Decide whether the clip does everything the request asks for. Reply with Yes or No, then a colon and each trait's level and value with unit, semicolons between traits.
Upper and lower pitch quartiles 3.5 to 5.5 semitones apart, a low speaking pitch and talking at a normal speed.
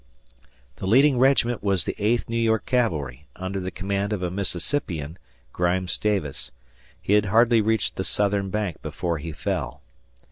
Yes: average, 3.8 semitones; low, 100 Hz; average, 155 wpm